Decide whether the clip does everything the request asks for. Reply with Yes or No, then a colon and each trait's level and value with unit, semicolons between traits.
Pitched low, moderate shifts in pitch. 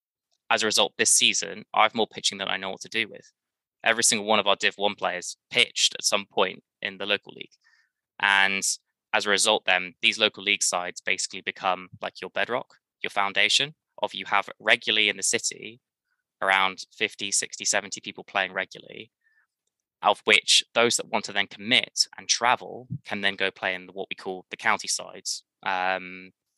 No: very low, 95 Hz; narrow, 1.9 semitones